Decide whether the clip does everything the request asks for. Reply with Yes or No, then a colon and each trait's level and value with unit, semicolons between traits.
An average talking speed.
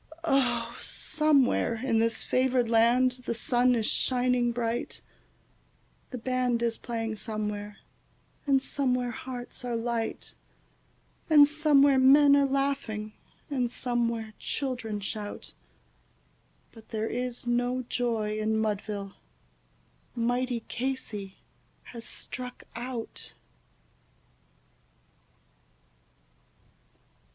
No: slow, 90 wpm